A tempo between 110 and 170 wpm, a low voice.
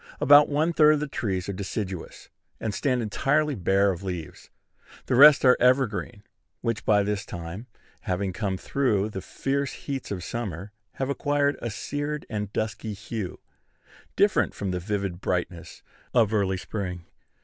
Yes: average, 155 wpm; low, 105 Hz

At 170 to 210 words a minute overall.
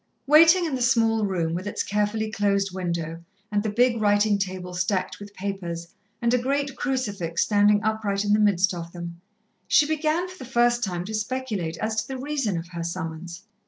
Yes: average, 195 wpm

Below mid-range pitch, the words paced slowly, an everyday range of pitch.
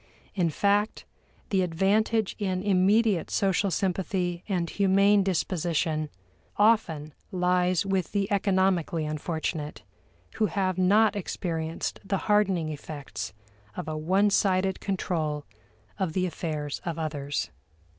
No: medium, 185 Hz; slow, 115 wpm; average, 3.5 semitones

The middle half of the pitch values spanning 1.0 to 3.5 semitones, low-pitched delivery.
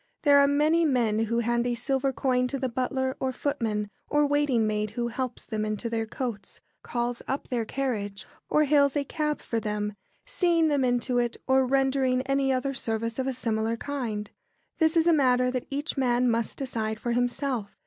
No: average, 3.2 semitones; very high, 250 Hz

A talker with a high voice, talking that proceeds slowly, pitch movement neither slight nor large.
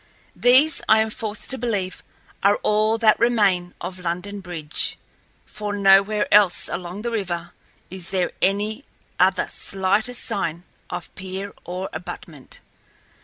Yes: high, 200 Hz; slow, 130 wpm; average, 3.0 semitones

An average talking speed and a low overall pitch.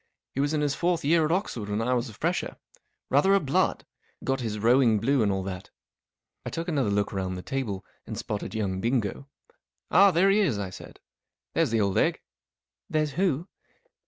No: fast, 210 wpm; low, 125 Hz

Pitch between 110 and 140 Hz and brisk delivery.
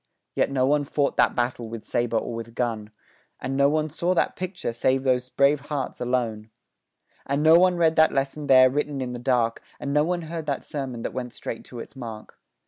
Yes: low, 135 Hz; fast, 215 wpm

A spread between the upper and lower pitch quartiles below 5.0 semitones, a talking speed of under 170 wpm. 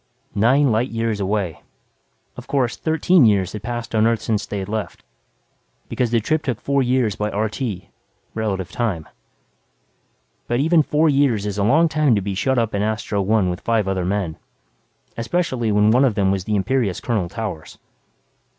No: average, 4.0 semitones; average, 180 wpm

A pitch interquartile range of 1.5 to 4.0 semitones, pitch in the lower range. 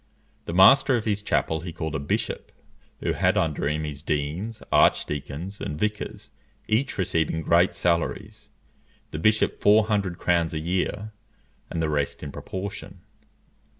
No: average, 4.9 semitones; very low, 85 Hz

